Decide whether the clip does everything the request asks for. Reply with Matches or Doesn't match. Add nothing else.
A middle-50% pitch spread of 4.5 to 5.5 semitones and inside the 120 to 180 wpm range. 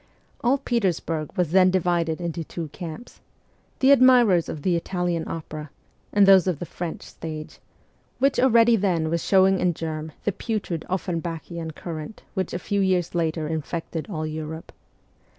Doesn't match